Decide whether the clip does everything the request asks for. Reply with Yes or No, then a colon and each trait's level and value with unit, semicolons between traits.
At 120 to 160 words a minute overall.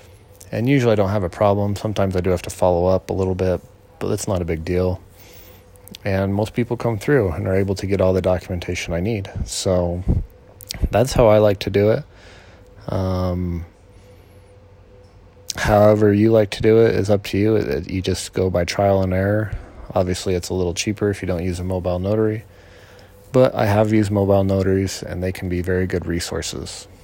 No: average, 200 wpm